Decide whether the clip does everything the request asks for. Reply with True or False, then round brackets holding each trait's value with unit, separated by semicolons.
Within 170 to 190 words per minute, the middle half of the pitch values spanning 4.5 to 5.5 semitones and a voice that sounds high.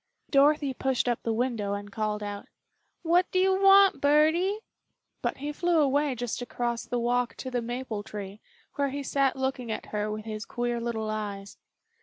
True (180 wpm; 4.9 semitones; 245 Hz)